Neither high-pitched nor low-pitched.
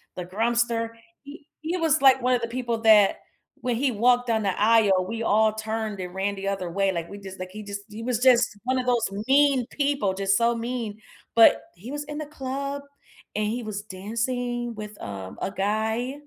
No: high, 225 Hz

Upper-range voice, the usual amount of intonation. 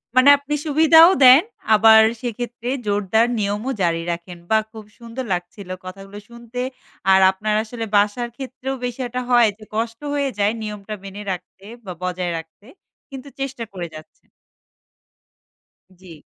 Yes: high, 220 Hz; average, 4.2 semitones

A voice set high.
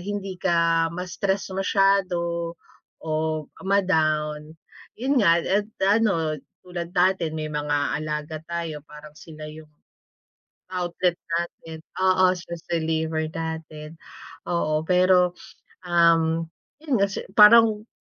No: medium, 170 Hz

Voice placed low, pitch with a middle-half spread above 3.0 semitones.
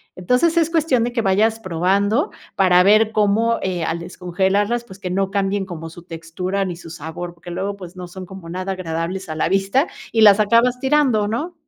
No: high, 195 Hz; average, 3.9 semitones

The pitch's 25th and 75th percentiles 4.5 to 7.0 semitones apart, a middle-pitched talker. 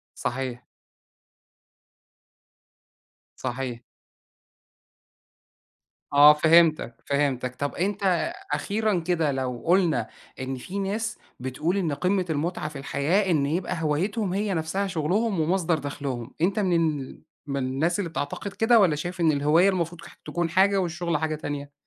Yes: average, 4.8 semitones; medium, 165 Hz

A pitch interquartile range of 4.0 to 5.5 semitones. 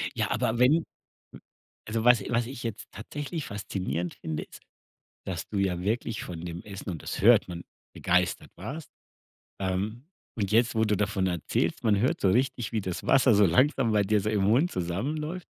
Yes: average, 4.6 semitones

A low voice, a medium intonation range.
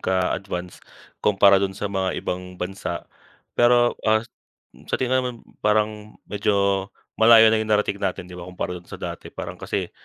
Yes: low, 100 Hz; average, 3.0 semitones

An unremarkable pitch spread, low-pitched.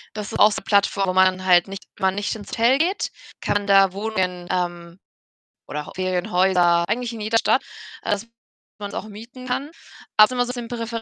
No: average, 3.7 semitones; high, 205 Hz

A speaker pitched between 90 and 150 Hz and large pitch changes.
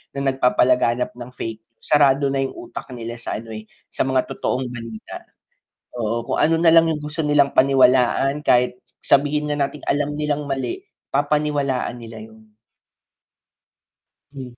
No: low, 135 Hz; average, 3.6 semitones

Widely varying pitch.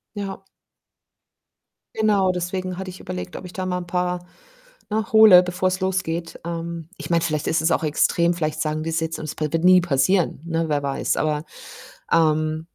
No: average, 2.8 semitones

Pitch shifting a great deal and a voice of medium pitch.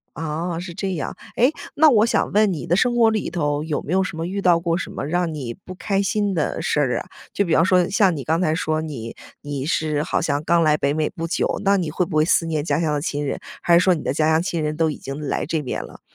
No: average, 3.4 semitones; medium, 165 Hz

